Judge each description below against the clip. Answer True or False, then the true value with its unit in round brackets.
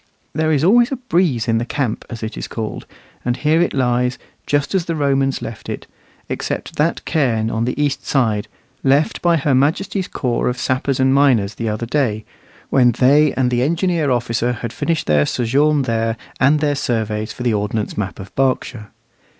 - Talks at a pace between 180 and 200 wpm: True (190 wpm)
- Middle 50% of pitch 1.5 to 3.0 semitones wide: False (4.4 semitones)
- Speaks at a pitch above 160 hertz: False (130 Hz)